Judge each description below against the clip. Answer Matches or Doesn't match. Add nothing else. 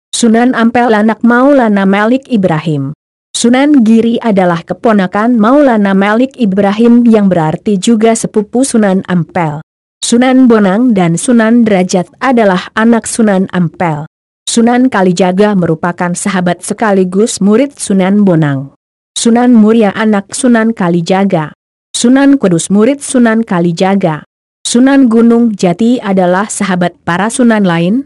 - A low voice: Doesn't match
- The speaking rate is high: Doesn't match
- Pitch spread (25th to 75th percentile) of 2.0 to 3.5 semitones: Doesn't match